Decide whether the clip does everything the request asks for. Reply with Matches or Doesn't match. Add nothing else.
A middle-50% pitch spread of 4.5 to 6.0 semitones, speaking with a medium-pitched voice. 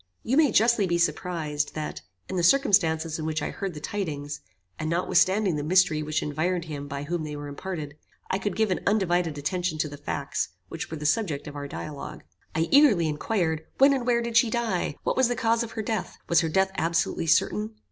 Matches